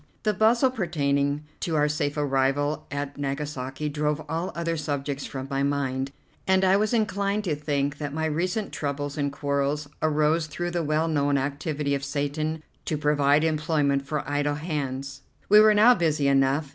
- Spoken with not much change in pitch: Yes, narrow, 2.3 semitones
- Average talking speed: Yes, average, 170 wpm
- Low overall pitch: No, medium, 150 Hz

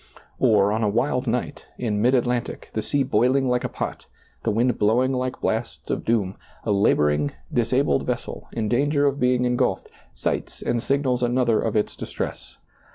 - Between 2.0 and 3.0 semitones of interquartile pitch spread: Yes, average, 2.7 semitones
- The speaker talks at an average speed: Yes, average, 175 wpm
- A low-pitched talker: Yes, low, 120 Hz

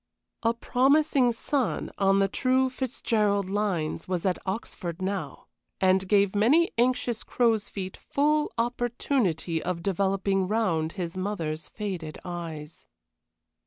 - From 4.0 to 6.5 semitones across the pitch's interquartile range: Yes, average, 4.6 semitones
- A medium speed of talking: No, slow, 120 wpm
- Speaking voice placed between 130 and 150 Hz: No, high, 200 Hz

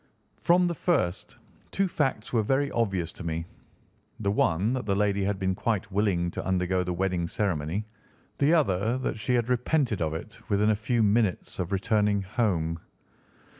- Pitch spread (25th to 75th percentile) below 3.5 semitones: No, average, 4.4 semitones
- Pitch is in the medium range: No, low, 105 Hz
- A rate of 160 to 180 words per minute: Yes, average, 170 wpm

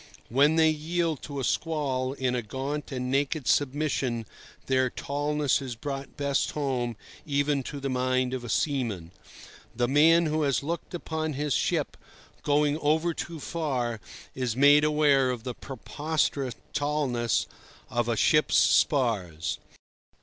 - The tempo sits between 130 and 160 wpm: Yes, average, 140 wpm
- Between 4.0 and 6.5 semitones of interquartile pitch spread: No, average, 3.0 semitones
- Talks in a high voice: No, medium, 140 Hz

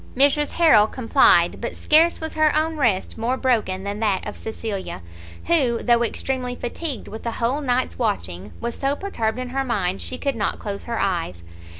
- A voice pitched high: Yes, high, 235 Hz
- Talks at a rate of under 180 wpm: No, average, 185 wpm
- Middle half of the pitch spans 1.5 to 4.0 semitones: No, average, 4.6 semitones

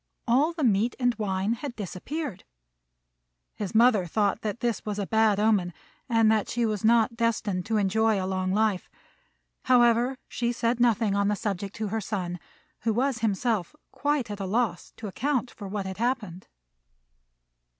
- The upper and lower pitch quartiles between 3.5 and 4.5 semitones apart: No, average, 3.0 semitones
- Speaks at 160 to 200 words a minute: Yes, average, 165 wpm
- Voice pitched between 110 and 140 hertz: No, high, 220 Hz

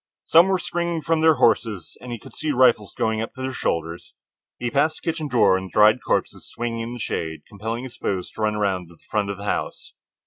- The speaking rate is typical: No, fast, 235 wpm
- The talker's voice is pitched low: Yes, low, 115 Hz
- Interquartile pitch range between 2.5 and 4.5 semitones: No, wide, 5.5 semitones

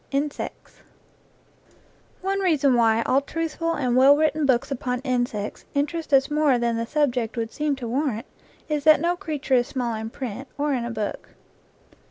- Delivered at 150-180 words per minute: Yes, average, 175 wpm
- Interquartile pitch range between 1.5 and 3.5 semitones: No, average, 4.0 semitones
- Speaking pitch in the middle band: No, very high, 270 Hz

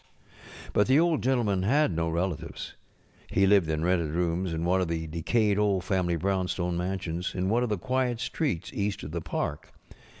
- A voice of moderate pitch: No, very low, 95 Hz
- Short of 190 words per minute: Yes, average, 180 wpm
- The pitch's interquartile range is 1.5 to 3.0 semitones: No, average, 3.8 semitones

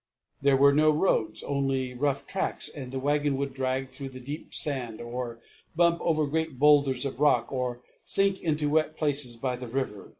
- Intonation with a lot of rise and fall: No, average, 2.8 semitones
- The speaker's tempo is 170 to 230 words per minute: Yes, average, 185 wpm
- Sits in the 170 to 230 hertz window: No, medium, 140 Hz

